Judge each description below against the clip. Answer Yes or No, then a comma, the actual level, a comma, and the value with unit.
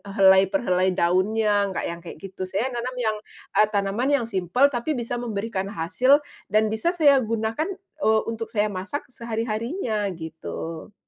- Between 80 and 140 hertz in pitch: No, high, 220 Hz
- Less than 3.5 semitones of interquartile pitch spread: No, average, 3.8 semitones